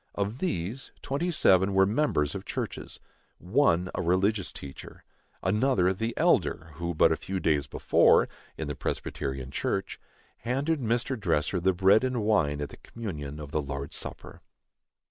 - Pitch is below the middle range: Yes, very low, 95 Hz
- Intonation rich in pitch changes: Yes, wide, 7.0 semitones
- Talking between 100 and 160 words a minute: Yes, average, 155 wpm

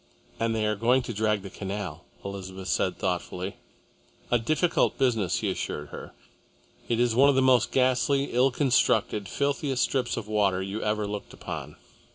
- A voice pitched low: Yes, low, 110 Hz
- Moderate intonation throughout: Yes, average, 4.3 semitones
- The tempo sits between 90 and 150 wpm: No, average, 170 wpm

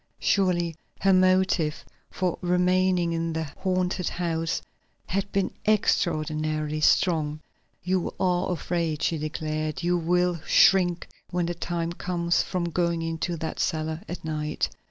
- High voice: No, medium, 170 Hz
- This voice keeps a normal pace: No, slow, 130 wpm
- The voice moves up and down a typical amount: No, narrow, 2.2 semitones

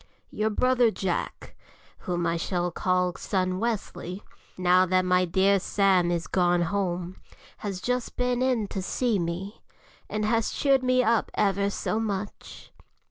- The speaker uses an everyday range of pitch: Yes, average, 3.5 semitones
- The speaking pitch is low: No, high, 195 Hz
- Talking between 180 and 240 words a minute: No, average, 145 wpm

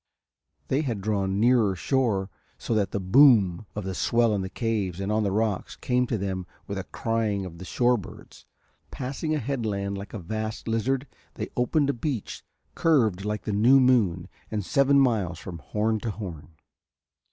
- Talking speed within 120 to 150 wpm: No, average, 180 wpm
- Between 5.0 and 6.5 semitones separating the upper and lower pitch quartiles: No, average, 4.2 semitones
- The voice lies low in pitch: Yes, low, 110 Hz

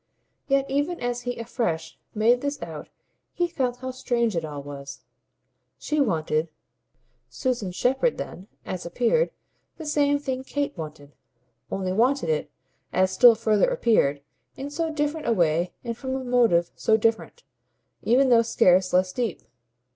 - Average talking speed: Yes, average, 150 wpm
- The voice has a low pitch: No, high, 235 Hz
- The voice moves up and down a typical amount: No, wide, 7.0 semitones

